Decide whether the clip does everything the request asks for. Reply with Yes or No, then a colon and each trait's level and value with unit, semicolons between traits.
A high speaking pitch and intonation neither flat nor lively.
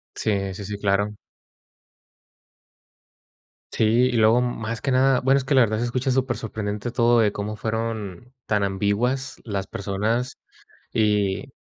No: low, 110 Hz; average, 3.3 semitones